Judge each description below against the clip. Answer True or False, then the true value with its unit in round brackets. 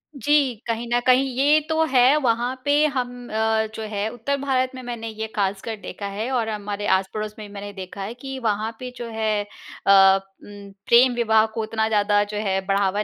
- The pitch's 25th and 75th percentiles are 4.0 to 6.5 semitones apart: False (3.5 semitones)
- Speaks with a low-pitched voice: False (220 Hz)